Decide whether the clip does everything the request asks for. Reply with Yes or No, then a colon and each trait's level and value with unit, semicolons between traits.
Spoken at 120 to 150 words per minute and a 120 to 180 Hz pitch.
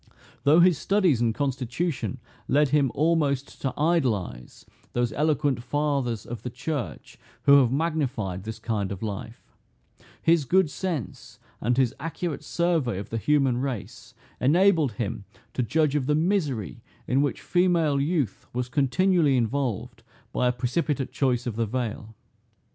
Yes: average, 145 wpm; low, 135 Hz